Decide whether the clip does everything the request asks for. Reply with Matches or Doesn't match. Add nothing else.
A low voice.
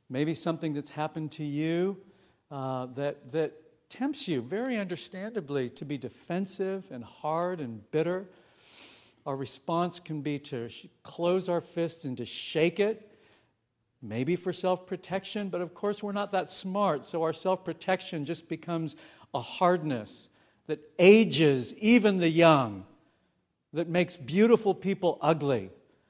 Doesn't match